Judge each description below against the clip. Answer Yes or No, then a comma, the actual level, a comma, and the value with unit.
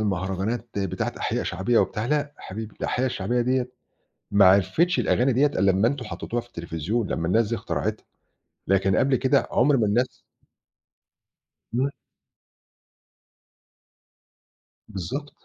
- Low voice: Yes, low, 115 Hz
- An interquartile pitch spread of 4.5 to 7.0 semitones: Yes, average, 4.9 semitones